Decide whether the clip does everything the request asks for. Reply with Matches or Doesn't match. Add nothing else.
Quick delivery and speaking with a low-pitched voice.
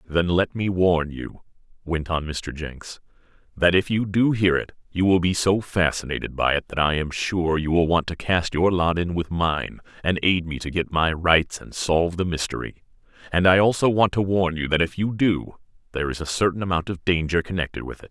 Matches